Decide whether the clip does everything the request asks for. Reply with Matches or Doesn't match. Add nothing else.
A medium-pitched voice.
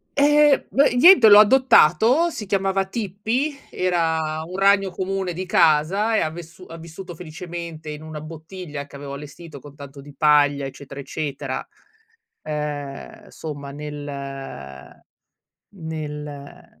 Matches